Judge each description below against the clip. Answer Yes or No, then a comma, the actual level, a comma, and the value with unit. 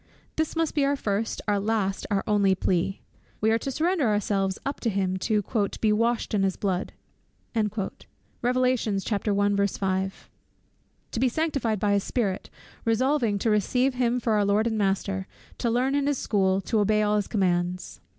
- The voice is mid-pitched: No, high, 210 Hz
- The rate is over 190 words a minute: No, average, 160 wpm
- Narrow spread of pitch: No, average, 3.6 semitones